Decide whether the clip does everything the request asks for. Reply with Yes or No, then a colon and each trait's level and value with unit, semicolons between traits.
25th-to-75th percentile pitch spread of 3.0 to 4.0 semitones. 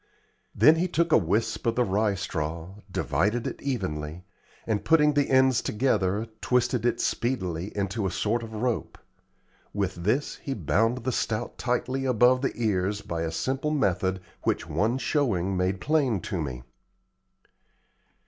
No: wide, 5.6 semitones